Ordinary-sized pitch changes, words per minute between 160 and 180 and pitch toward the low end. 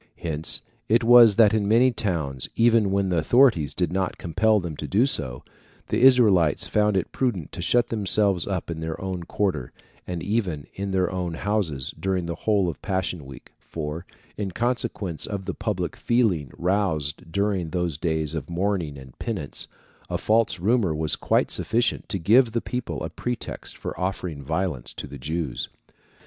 Yes: average, 4.9 semitones; average, 175 wpm; very low, 95 Hz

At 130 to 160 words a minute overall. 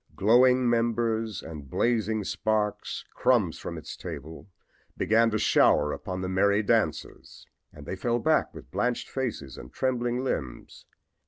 Yes: average, 140 wpm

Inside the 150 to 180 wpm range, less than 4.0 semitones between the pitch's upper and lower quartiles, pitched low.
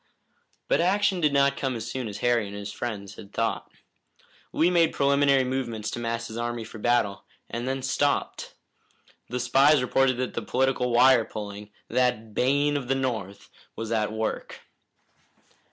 Yes: average, 160 wpm; average, 3.3 semitones; low, 125 Hz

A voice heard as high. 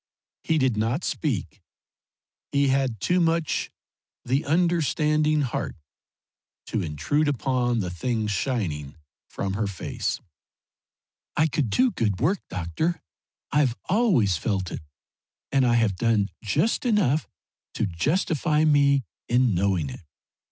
No: low, 130 Hz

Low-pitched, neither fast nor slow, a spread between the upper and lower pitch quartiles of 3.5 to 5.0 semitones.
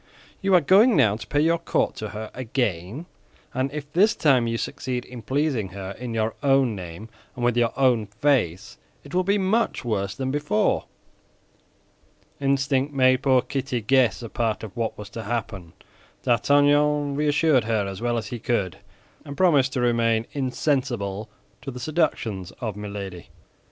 Yes: low, 125 Hz; average, 165 wpm; average, 4.7 semitones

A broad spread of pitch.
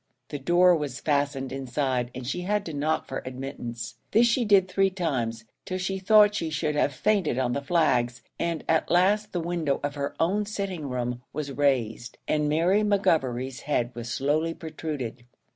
Yes: wide, 5.7 semitones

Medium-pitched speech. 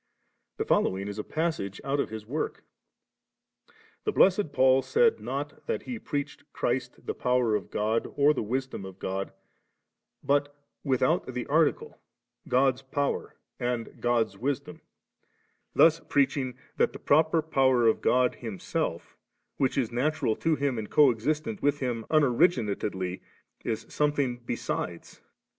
No: low, 130 Hz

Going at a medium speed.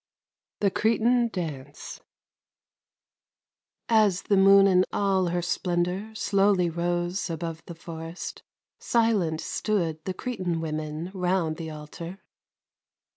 No: slow, 105 wpm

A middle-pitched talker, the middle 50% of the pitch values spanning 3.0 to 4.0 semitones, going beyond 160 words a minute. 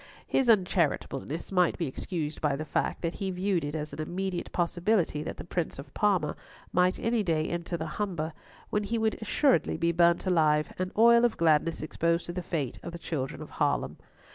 Yes: medium, 170 Hz; average, 3.6 semitones; average, 195 wpm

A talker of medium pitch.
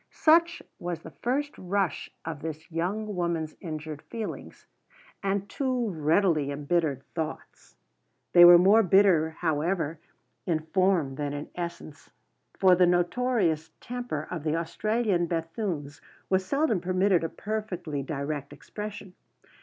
Yes: medium, 175 Hz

